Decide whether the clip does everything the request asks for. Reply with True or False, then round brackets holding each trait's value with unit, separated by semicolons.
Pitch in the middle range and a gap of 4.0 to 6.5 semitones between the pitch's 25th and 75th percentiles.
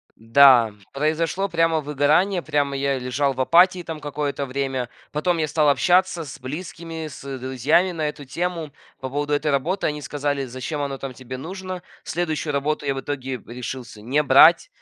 False (145 Hz; 3.5 semitones)